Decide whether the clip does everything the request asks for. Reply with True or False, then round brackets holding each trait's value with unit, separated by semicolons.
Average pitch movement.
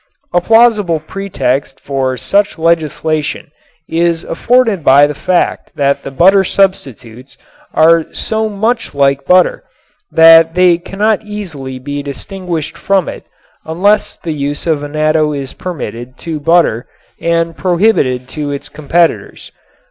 True (4.5 semitones)